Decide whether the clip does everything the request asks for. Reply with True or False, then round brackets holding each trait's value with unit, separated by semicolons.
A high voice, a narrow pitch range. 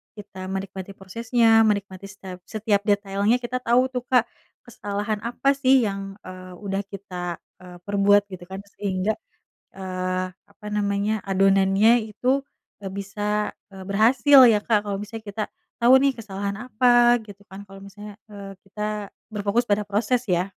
True (205 Hz; 2.3 semitones)